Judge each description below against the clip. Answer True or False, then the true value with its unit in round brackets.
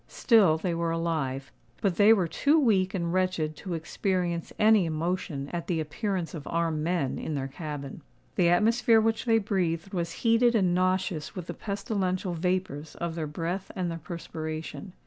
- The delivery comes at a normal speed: True (170 wpm)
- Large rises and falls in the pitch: False (3.3 semitones)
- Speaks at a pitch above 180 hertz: False (175 Hz)